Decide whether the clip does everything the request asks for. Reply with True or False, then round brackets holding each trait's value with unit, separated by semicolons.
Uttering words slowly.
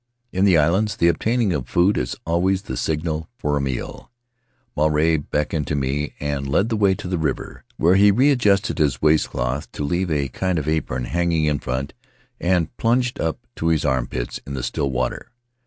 False (190 wpm)